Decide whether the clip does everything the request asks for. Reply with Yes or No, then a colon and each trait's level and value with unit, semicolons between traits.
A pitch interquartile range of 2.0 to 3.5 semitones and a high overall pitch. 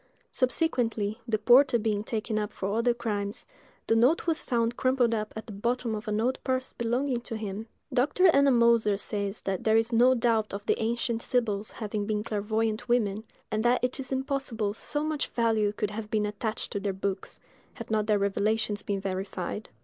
Yes: average, 2.7 semitones; high, 225 Hz